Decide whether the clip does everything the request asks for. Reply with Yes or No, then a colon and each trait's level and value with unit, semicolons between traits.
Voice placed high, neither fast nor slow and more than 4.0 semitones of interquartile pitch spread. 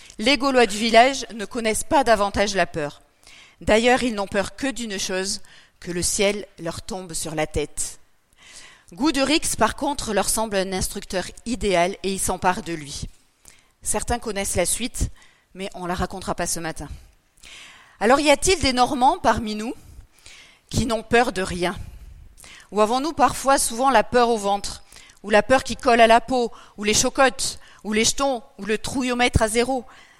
Yes: high, 215 Hz; average, 175 wpm; average, 4.7 semitones